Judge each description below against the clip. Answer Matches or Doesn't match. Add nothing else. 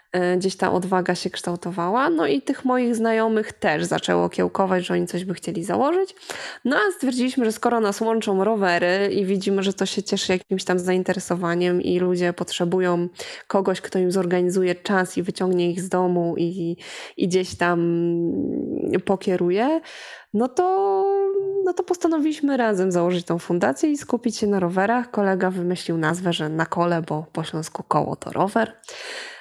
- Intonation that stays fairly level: Doesn't match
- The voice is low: Doesn't match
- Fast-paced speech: Matches